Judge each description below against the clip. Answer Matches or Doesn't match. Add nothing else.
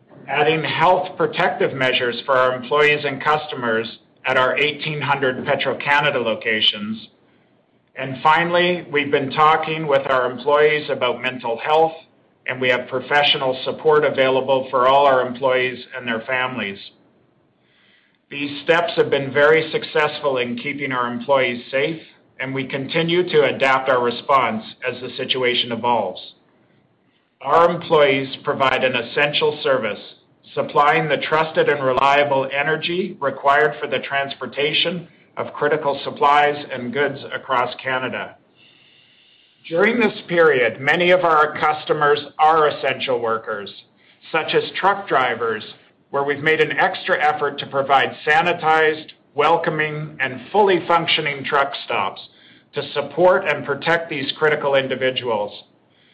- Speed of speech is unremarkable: Doesn't match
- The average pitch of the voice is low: Doesn't match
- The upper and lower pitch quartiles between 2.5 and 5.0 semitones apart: Matches